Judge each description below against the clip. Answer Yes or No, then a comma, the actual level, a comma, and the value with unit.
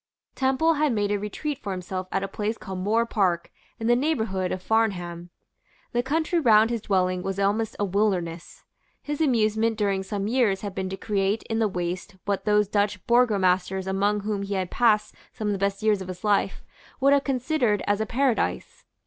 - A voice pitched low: No, high, 205 Hz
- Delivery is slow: No, average, 195 wpm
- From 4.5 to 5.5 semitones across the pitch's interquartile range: No, average, 3.1 semitones